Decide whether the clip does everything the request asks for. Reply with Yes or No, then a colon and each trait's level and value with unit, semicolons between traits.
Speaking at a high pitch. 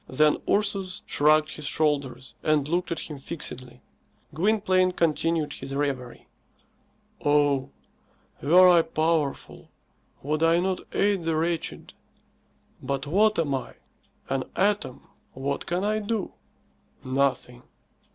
No: medium, 155 Hz